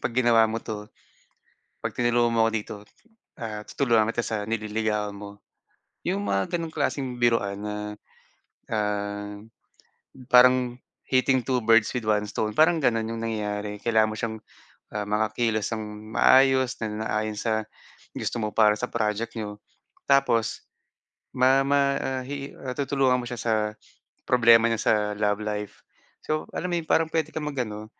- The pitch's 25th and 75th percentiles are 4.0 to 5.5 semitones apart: No, average, 3.2 semitones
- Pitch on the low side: Yes, low, 115 Hz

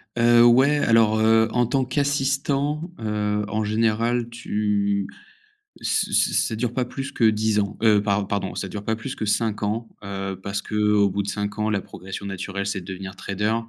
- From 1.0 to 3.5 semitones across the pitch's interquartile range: Yes, average, 2.8 semitones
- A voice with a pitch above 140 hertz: No, low, 110 Hz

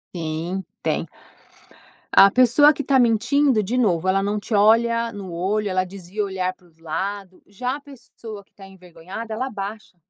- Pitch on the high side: Yes, high, 200 Hz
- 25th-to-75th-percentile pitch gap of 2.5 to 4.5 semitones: Yes, average, 3.8 semitones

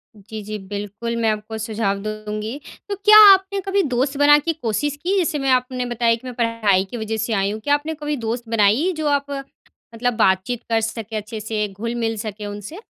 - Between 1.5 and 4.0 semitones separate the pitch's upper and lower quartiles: No, average, 4.8 semitones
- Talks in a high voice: Yes, high, 230 Hz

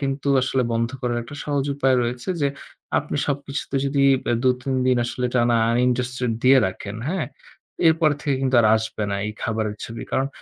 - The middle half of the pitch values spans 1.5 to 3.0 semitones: Yes, average, 2.7 semitones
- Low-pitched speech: Yes, low, 130 Hz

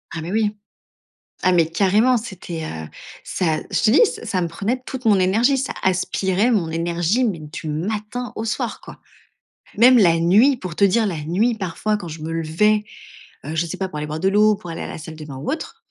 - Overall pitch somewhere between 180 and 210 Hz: Yes, high, 190 Hz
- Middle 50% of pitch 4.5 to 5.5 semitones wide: Yes, average, 4.9 semitones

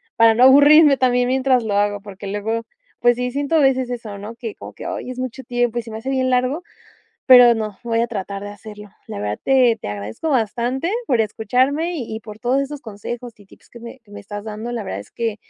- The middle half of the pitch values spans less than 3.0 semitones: No, average, 3.6 semitones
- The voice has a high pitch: Yes, high, 235 Hz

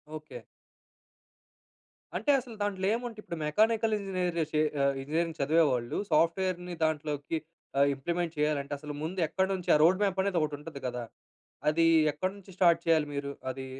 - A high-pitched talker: No, medium, 165 Hz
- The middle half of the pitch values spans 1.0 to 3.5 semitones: No, average, 4.0 semitones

